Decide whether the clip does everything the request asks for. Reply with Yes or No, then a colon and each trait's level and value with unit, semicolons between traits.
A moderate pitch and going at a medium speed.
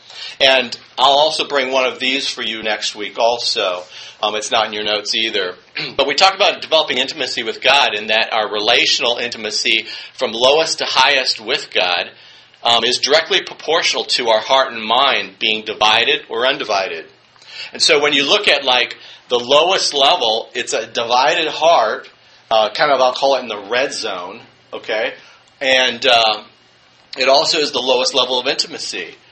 No: low, 120 Hz; average, 175 wpm